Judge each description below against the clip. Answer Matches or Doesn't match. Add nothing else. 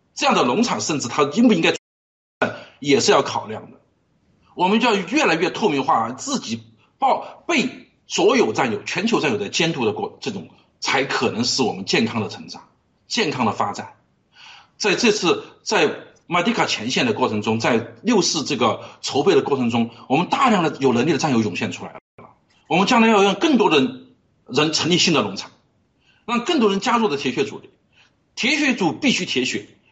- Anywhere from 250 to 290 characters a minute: Matches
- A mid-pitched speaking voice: Matches